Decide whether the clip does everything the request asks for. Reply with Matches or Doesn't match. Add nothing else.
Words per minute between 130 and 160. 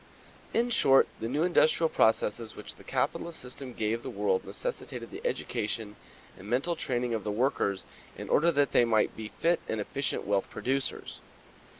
Doesn't match